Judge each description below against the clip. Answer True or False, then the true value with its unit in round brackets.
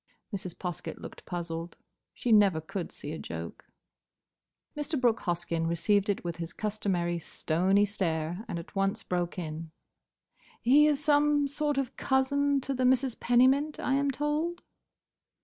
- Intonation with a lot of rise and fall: True (8.2 semitones)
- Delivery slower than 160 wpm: True (150 wpm)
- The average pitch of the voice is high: True (205 Hz)